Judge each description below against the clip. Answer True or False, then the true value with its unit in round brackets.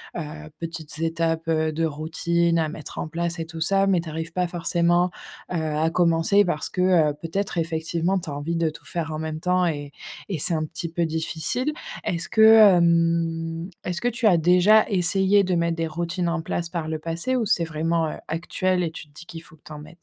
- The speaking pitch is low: False (170 Hz)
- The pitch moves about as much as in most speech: False (1.8 semitones)